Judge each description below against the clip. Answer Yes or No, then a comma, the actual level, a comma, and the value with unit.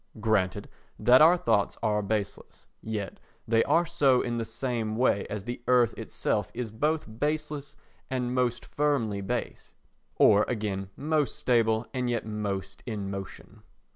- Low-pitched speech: Yes, low, 115 Hz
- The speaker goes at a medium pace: Yes, average, 145 wpm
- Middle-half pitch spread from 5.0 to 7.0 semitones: No, average, 3.7 semitones